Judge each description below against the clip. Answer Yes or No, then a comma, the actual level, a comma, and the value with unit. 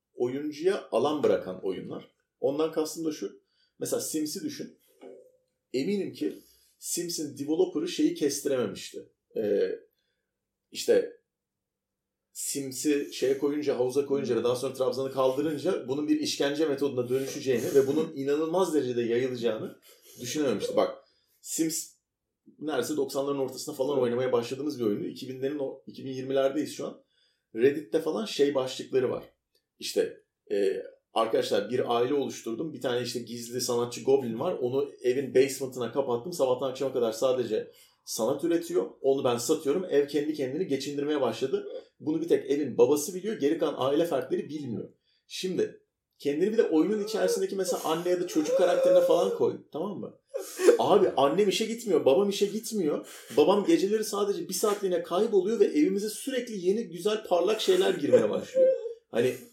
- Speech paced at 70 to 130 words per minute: No, fast, 140 wpm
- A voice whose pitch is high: Yes, high, 200 Hz